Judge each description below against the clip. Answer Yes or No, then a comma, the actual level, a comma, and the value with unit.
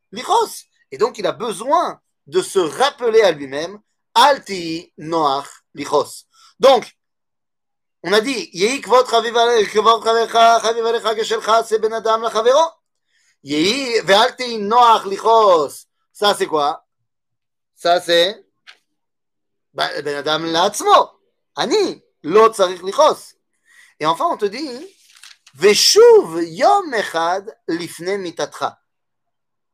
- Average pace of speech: No, slow, 105 wpm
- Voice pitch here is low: No, high, 225 Hz